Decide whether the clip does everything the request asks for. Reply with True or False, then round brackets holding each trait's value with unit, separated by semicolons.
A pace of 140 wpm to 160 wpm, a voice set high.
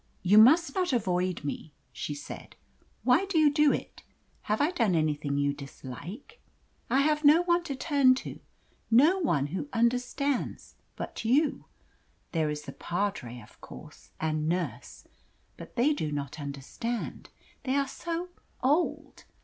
True (150 wpm; 235 Hz)